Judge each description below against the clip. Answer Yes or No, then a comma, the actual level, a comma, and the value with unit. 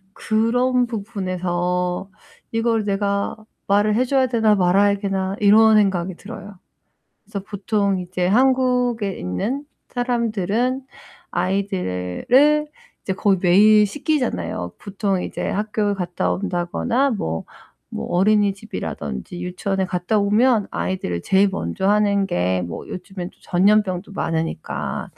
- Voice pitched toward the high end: Yes, high, 200 Hz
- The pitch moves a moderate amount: Yes, average, 3.4 semitones